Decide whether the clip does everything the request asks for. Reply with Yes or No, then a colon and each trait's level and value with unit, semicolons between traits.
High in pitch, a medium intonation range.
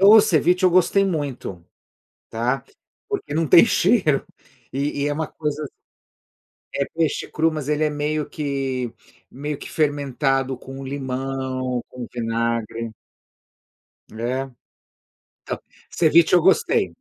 No: medium, 145 Hz; average, 3.5 semitones